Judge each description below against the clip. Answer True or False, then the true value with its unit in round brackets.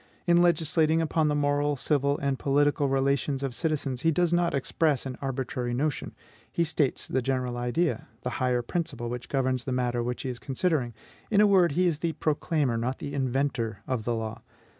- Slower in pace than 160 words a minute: False (190 wpm)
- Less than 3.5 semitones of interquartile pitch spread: False (3.8 semitones)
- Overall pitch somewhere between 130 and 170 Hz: True (140 Hz)